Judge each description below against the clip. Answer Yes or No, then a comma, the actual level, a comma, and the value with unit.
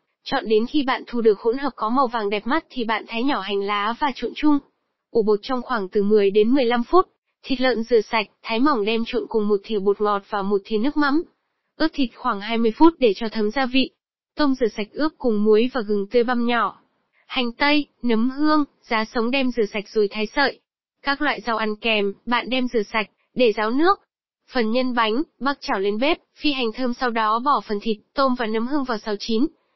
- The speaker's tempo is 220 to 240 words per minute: Yes, average, 235 wpm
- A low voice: No, high, 235 Hz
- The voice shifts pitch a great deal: No, average, 4.0 semitones